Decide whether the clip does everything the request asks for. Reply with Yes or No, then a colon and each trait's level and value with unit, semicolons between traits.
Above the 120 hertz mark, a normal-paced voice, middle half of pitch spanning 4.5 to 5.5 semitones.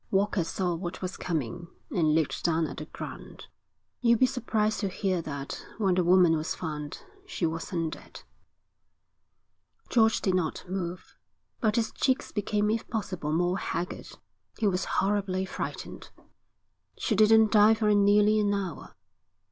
No: high, 190 Hz; average, 150 wpm; average, 3.9 semitones